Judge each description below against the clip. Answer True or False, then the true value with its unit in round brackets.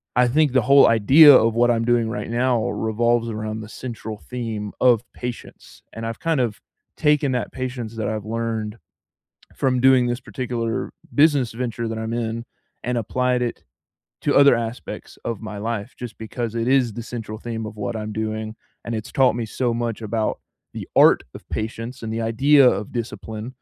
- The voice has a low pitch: True (115 Hz)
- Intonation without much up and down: True (2.1 semitones)